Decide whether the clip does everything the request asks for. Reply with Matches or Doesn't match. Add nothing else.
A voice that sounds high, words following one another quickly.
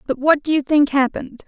Matches